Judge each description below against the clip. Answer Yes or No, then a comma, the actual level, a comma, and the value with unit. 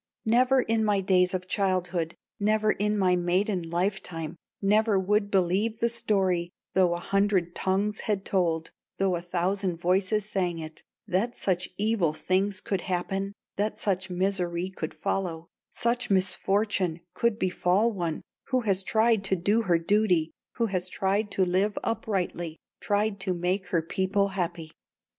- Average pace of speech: Yes, average, 155 wpm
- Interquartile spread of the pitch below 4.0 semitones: Yes, average, 2.7 semitones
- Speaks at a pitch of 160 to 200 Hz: Yes, high, 190 Hz